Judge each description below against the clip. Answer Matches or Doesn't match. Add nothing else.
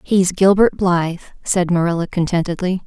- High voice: Doesn't match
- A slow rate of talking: Matches